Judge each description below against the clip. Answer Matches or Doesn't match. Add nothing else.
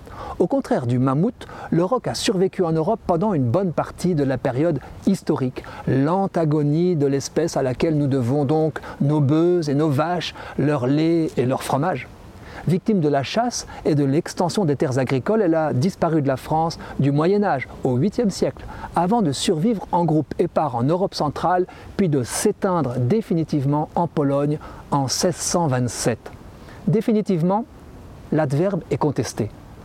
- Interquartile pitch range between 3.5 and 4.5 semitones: Doesn't match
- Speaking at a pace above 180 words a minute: Doesn't match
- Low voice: Doesn't match